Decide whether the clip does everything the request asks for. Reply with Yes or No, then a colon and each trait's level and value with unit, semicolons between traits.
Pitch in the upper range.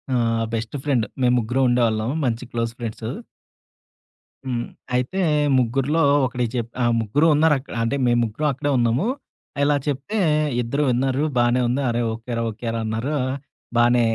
No: low, 120 Hz